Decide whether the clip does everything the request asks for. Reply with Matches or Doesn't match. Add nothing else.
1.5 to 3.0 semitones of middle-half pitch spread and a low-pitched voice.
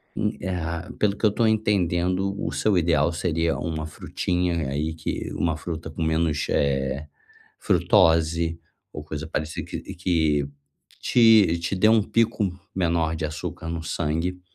Matches